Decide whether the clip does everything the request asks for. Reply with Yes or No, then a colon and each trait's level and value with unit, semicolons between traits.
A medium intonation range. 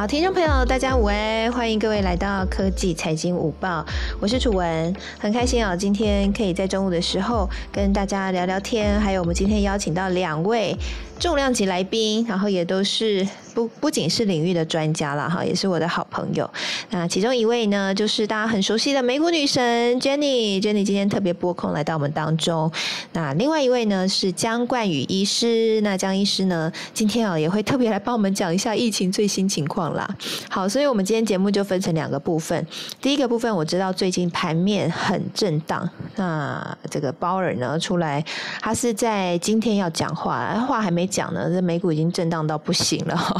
Yes: average, 4.2 semitones